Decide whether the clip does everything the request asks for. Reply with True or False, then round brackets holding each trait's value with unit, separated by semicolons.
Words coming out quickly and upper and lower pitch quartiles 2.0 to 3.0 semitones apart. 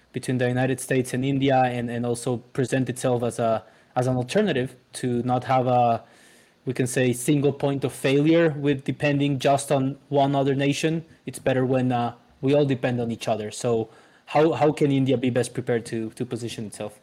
False (195 wpm; 2.6 semitones)